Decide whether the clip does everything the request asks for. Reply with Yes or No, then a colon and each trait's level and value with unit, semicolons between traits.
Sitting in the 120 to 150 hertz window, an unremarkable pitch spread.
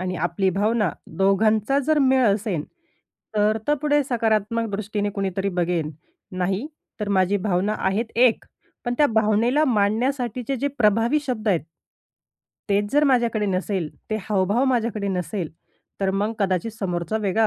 No: high, 210 Hz; average, 3.5 semitones